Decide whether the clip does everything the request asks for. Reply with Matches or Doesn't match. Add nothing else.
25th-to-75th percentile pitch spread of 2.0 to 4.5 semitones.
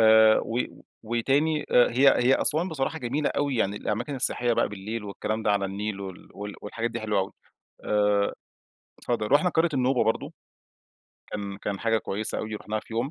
Matches